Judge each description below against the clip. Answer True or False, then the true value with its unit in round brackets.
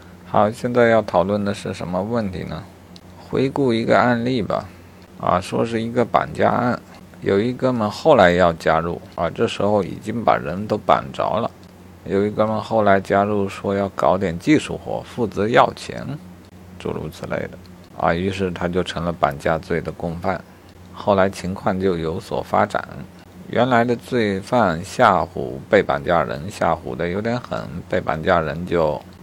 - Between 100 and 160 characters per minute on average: False (240 characters per minute)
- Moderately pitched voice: False (95 Hz)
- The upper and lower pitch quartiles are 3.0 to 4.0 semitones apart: True (3.4 semitones)